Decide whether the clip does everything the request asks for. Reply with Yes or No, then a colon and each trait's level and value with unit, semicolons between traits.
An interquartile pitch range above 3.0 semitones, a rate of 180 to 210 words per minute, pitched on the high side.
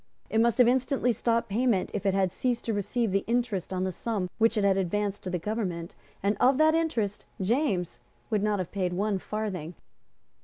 Yes: average, 3.8 semitones; average, 200 wpm; high, 210 Hz